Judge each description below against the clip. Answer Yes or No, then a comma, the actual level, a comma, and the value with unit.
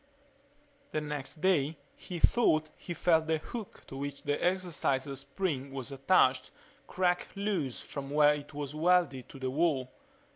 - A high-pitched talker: No, medium, 150 Hz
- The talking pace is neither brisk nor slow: Yes, average, 150 wpm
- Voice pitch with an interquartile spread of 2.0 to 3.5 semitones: No, average, 4.3 semitones